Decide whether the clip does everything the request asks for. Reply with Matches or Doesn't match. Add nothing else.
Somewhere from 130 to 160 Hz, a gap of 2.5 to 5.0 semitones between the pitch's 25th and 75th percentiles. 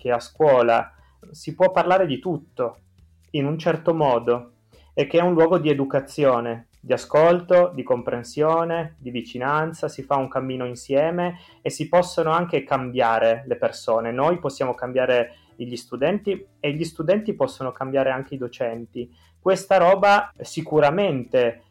Doesn't match